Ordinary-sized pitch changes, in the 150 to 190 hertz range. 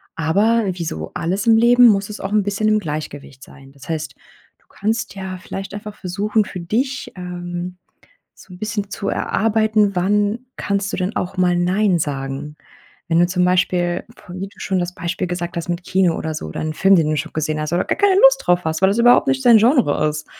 Yes: average, 3.7 semitones; medium, 185 Hz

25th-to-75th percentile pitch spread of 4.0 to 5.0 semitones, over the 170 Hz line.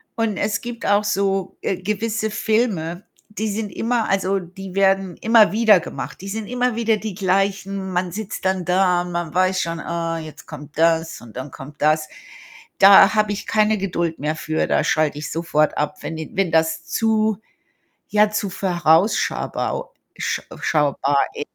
Yes: average, 4.4 semitones; high, 190 Hz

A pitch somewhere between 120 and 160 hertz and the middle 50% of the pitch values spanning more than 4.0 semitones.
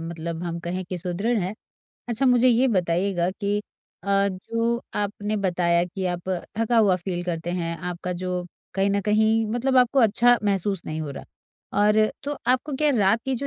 No: high, 195 Hz; average, 4.6 semitones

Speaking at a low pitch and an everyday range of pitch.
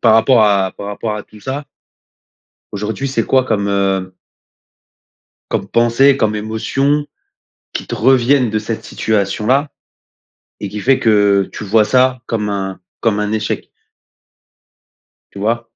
Yes: low, 110 Hz; average, 3.8 semitones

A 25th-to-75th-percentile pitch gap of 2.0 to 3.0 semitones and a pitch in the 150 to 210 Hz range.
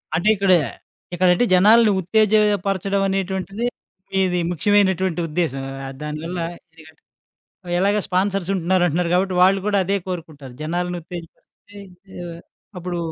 Yes: narrow, 2.6 semitones; medium, 185 Hz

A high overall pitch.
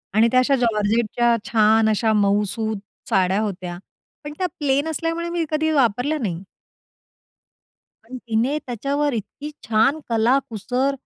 Yes: high, 235 Hz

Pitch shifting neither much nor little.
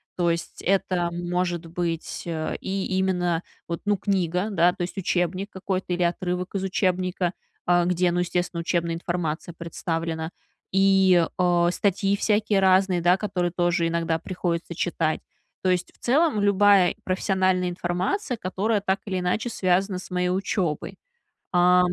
No: narrow, 1.8 semitones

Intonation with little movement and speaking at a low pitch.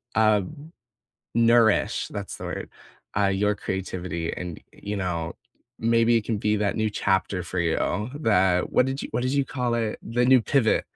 No: average, 3.8 semitones; low, 105 Hz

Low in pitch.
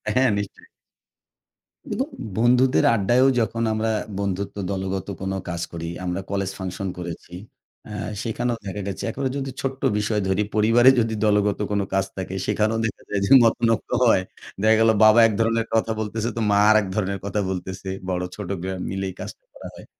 Yes: low, 105 Hz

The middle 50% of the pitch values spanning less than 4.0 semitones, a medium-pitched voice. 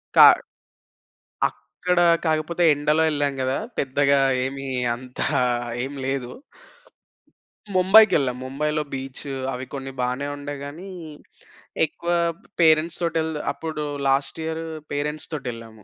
Yes: average, 3.0 semitones; medium, 145 Hz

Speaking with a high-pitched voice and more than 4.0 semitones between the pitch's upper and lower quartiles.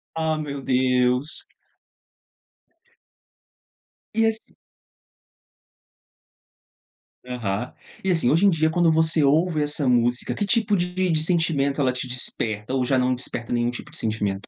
No: medium, 140 Hz; average, 4.7 semitones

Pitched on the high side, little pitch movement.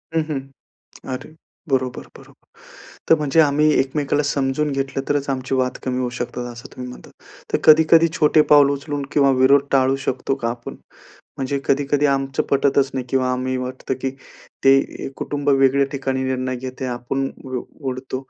No: low, 135 Hz; narrow, 1.6 semitones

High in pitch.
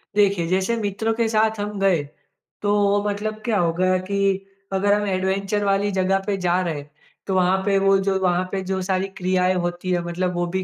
Yes: high, 195 Hz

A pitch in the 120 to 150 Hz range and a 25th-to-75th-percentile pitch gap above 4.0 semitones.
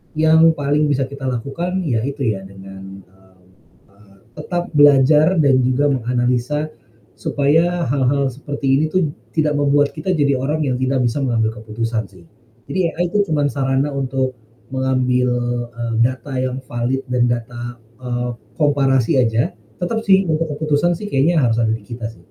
No: low, 135 Hz; average, 3.6 semitones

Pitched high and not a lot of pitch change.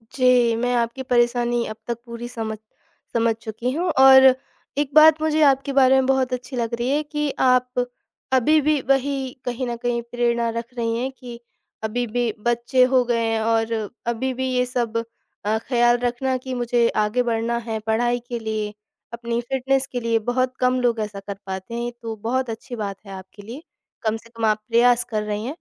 Yes: high, 240 Hz; narrow, 2.0 semitones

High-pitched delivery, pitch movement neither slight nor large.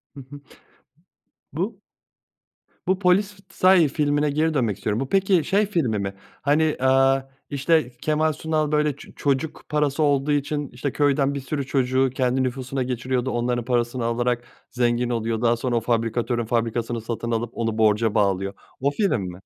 No: low, 130 Hz; average, 4.0 semitones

